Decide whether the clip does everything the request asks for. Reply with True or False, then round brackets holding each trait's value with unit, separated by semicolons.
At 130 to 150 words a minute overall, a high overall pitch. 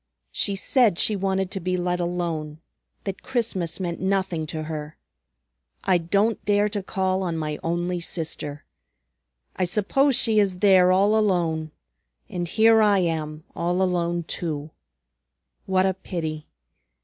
False (140 wpm; 180 Hz)